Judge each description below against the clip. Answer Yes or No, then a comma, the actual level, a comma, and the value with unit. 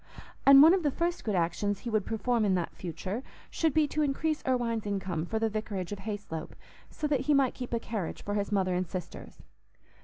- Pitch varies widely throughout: Yes, wide, 6.1 semitones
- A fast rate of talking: Yes, fast, 215 wpm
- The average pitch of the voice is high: Yes, high, 220 Hz